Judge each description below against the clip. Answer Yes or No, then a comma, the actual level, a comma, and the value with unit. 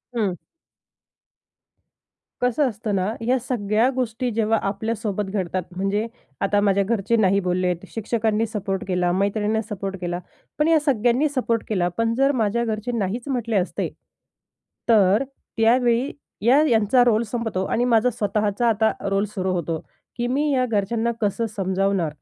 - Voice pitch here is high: Yes, high, 220 Hz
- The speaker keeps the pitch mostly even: No, average, 3.2 semitones